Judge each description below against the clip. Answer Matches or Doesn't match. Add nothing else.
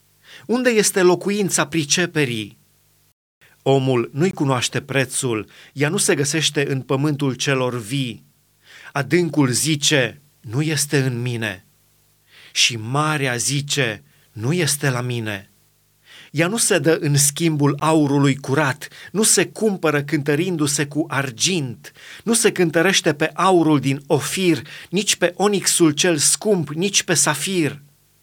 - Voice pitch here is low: Doesn't match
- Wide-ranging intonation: Doesn't match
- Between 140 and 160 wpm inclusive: Doesn't match